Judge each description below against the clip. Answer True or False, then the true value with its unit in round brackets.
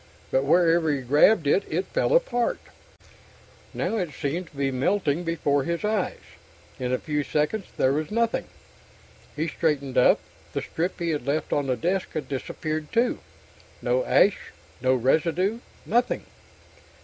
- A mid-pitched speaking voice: True (160 Hz)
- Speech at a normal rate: True (150 wpm)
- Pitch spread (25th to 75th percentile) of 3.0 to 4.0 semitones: False (5.2 semitones)